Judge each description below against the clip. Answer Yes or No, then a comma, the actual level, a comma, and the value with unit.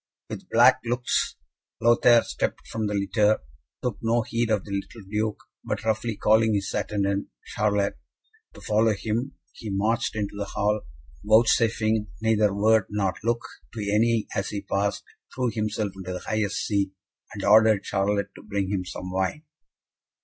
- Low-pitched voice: Yes, low, 105 Hz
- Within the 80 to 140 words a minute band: No, average, 155 wpm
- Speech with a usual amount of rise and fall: No, narrow, 1.9 semitones